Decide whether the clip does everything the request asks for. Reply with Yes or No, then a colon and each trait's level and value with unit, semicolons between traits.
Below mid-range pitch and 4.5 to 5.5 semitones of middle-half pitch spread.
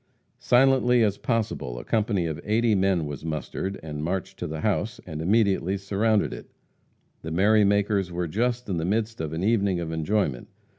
Yes: low, 100 Hz; average, 5.1 semitones